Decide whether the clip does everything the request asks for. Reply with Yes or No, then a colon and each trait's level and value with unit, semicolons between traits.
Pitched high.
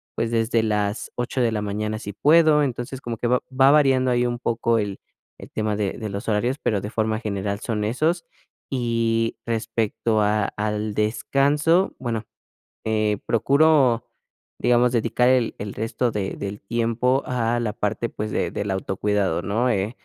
No: low, 115 Hz